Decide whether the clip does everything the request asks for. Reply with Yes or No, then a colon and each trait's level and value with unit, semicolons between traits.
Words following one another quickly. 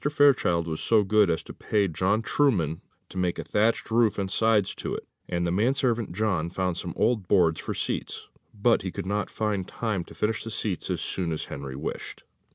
Yes: fast, 210 wpm